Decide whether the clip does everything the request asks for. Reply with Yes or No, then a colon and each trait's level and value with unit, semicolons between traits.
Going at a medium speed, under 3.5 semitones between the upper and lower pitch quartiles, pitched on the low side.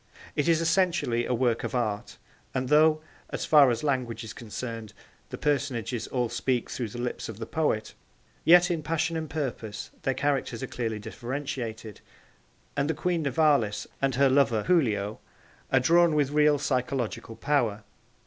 No: average, 160 wpm; average, 4.5 semitones; low, 130 Hz